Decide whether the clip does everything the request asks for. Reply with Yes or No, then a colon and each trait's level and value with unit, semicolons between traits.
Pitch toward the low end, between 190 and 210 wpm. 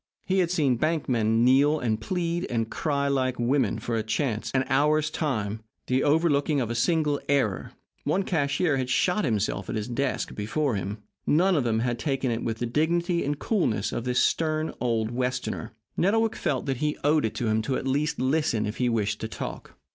Yes: low, 130 Hz; average, 200 wpm